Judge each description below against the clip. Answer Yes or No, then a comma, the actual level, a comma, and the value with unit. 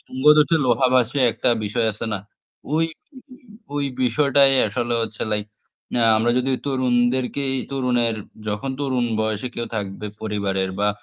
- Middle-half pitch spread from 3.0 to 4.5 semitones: Yes, average, 3.7 semitones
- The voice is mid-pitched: No, low, 120 Hz